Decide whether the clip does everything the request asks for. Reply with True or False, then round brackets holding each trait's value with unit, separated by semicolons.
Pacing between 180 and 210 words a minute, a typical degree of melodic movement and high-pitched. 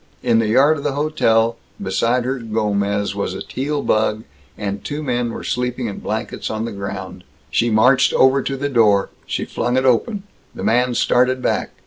False (185 wpm; 3.4 semitones; 120 Hz)